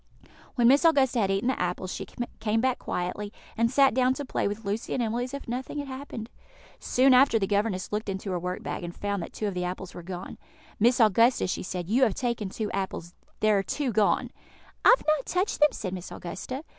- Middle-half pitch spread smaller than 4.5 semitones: No, average, 5.1 semitones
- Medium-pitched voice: No, high, 220 Hz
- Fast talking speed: Yes, fast, 230 wpm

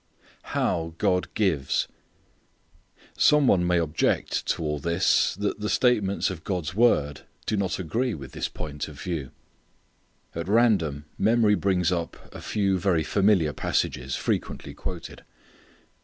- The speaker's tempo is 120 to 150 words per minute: Yes, slow, 135 wpm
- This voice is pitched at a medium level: No, very low, 90 Hz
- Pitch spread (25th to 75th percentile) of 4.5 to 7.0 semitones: Yes, average, 4.8 semitones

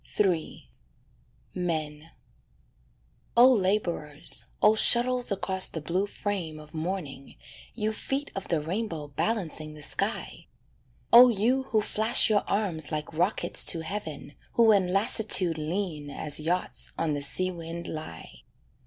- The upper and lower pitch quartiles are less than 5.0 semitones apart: No, average, 5.3 semitones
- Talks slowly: Yes, slow, 130 wpm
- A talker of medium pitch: Yes, medium, 180 Hz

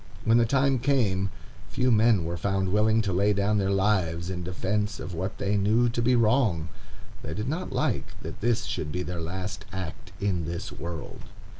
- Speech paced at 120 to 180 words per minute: No, average, 190 wpm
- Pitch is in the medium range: No, low, 100 Hz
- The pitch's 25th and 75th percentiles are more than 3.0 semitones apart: Yes, average, 4.0 semitones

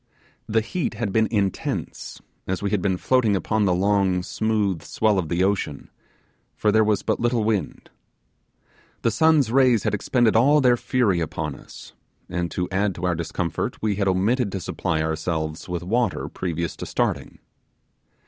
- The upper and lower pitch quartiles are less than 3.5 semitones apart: No, average, 3.8 semitones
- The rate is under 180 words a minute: Yes, average, 165 wpm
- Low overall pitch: Yes, low, 100 Hz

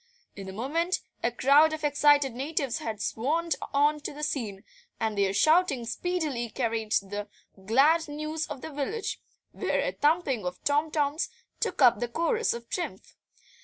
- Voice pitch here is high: Yes, very high, 285 Hz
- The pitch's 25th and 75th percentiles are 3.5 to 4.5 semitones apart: No, average, 5.2 semitones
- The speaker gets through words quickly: No, average, 165 wpm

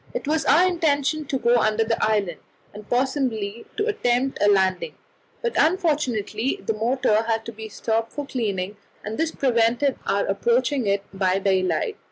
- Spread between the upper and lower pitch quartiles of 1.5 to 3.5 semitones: No, wide, 5.4 semitones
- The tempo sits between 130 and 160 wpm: No, average, 170 wpm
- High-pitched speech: Yes, high, 230 Hz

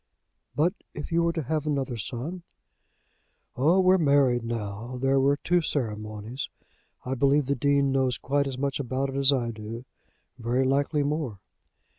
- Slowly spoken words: No, average, 160 wpm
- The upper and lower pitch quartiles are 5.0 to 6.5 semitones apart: No, average, 3.0 semitones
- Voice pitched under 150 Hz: Yes, low, 135 Hz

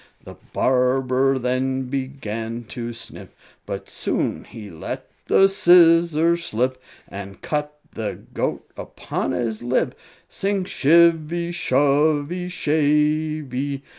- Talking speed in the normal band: No, slow, 105 wpm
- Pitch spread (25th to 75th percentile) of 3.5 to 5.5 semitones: Yes, average, 4.2 semitones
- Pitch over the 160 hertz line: No, medium, 140 Hz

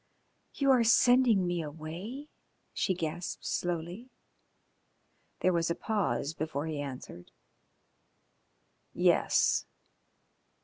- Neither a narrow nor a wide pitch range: No, wide, 6.1 semitones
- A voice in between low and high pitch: Yes, medium, 175 Hz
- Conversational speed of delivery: No, slow, 90 wpm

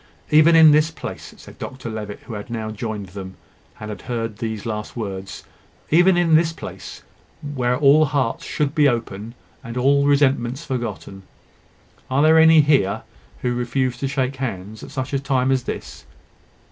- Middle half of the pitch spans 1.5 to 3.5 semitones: No, average, 4.7 semitones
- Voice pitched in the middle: No, low, 130 Hz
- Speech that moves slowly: No, average, 170 wpm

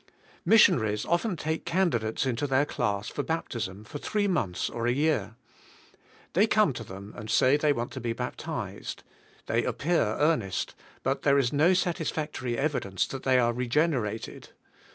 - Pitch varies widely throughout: Yes, wide, 5.8 semitones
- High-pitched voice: No, low, 135 Hz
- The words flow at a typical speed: Yes, average, 160 wpm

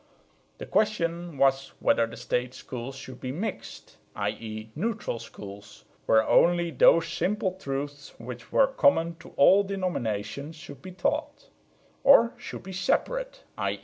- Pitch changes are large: Yes, wide, 7.4 semitones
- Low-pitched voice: No, medium, 160 Hz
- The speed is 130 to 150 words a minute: Yes, average, 140 wpm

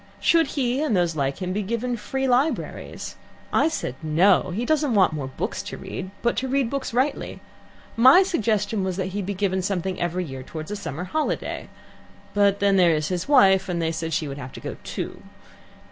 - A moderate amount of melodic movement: No, wide, 6.0 semitones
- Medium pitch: No, high, 195 Hz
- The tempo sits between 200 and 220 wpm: Yes, fast, 205 wpm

